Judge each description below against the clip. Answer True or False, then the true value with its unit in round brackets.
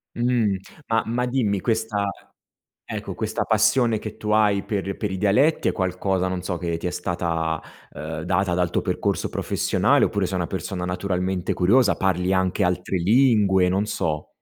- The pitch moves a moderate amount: True (3.1 semitones)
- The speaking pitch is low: True (95 Hz)